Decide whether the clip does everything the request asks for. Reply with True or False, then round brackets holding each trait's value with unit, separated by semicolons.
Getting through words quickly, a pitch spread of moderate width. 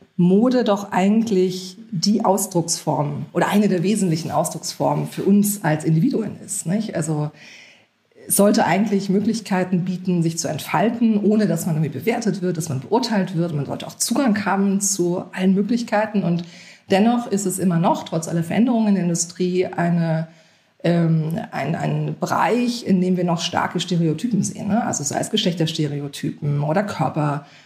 False (160 wpm; 3.6 semitones)